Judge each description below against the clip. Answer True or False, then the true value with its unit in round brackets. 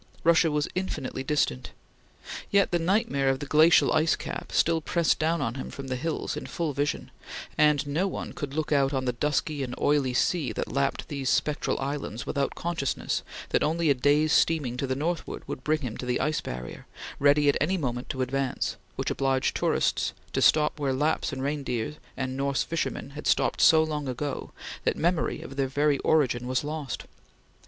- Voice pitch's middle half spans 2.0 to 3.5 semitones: True (2.8 semitones)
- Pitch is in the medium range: True (145 Hz)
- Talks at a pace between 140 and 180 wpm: False (190 wpm)